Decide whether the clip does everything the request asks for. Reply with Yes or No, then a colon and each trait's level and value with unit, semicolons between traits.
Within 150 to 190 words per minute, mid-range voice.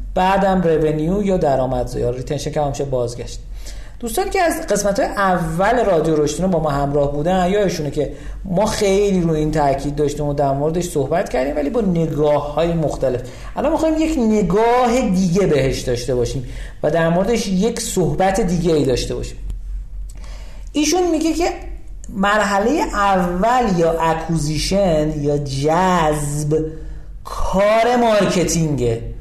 No: average, 140 wpm; medium, 165 Hz